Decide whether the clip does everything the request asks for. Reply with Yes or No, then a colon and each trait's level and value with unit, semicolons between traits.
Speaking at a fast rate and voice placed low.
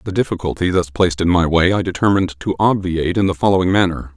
Yes: fast, 215 wpm; very low, 90 Hz